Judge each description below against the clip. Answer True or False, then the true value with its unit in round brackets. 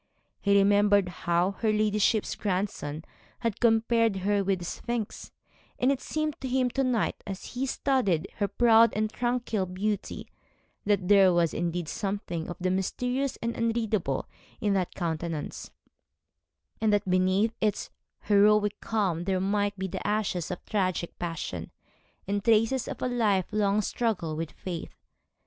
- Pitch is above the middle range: True (205 Hz)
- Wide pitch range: False (3.4 semitones)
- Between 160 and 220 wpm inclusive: False (150 wpm)